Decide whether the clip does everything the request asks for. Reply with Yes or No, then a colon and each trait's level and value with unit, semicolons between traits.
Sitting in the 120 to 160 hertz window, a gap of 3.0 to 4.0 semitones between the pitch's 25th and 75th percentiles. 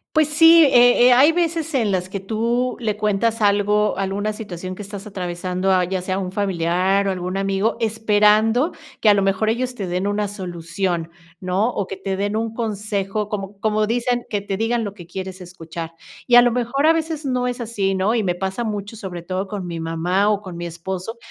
No: high, 205 Hz; average, 3.4 semitones